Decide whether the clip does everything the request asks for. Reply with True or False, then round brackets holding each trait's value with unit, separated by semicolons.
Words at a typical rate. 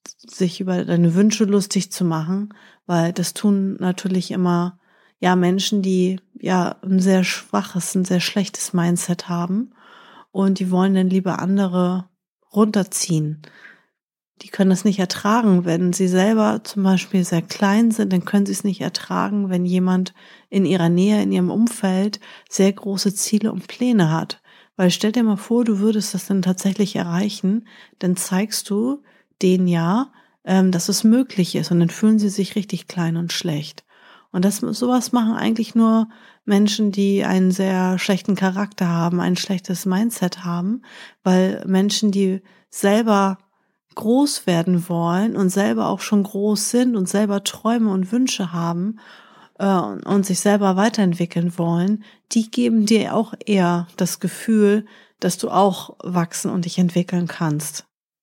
True (155 wpm)